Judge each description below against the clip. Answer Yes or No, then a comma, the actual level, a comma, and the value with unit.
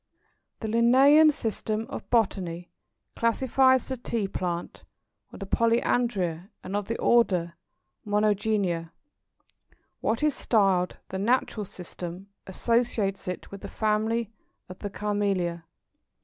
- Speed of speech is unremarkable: No, slow, 115 wpm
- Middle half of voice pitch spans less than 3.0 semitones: No, average, 3.9 semitones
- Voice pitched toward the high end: Yes, high, 210 Hz